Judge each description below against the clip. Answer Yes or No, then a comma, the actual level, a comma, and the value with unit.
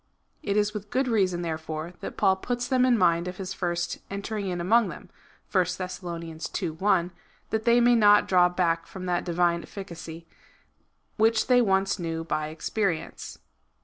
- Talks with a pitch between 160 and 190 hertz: Yes, medium, 185 Hz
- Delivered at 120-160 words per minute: No, average, 175 wpm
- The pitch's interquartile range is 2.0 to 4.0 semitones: Yes, average, 3.6 semitones